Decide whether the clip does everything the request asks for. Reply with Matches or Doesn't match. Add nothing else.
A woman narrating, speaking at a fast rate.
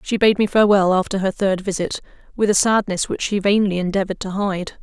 Matches